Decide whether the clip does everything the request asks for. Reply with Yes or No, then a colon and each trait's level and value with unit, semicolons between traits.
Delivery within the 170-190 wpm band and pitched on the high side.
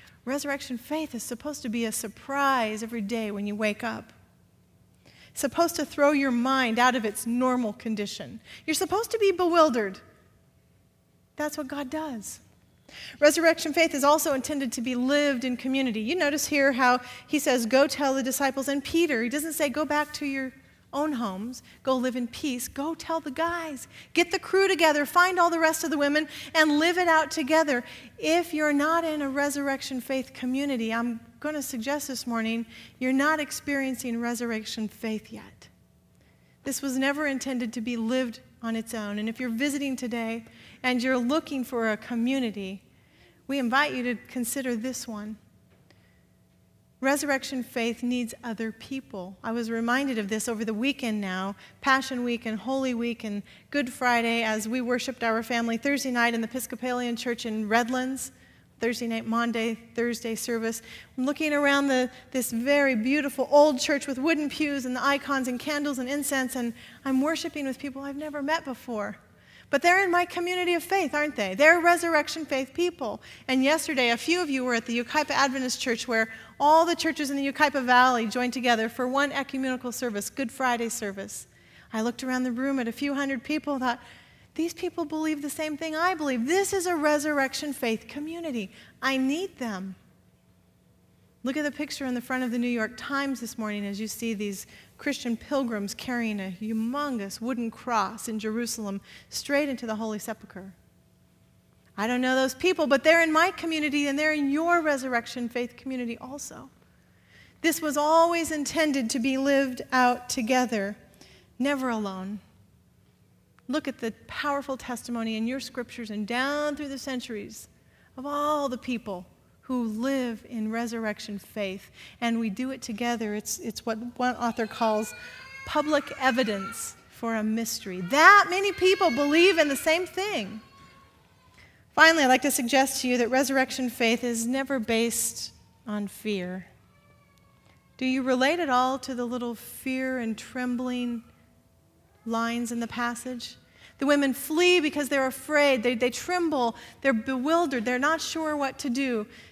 Yes: average, 175 wpm; very high, 260 Hz